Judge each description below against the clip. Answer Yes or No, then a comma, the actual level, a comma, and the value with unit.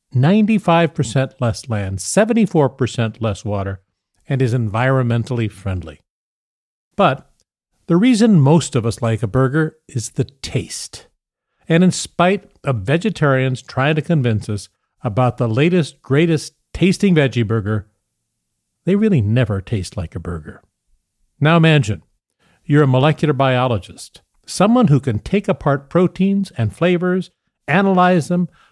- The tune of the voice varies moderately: No, wide, 7.0 semitones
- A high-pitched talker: No, low, 135 Hz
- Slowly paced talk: Yes, slow, 125 wpm